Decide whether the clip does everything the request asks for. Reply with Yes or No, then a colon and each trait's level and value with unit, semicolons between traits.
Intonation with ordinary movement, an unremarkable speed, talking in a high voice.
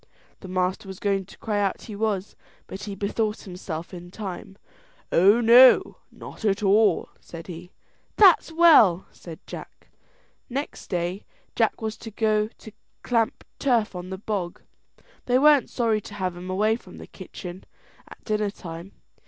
Yes: average, 3.3 semitones; average, 155 wpm; high, 200 Hz